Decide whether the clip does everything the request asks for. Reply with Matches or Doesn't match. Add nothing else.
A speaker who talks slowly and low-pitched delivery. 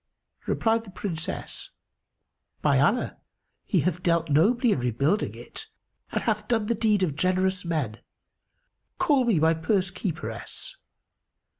Doesn't match